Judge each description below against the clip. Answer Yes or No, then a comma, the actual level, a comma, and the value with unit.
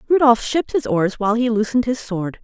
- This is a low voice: No, high, 235 Hz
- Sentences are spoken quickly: Yes, fast, 220 wpm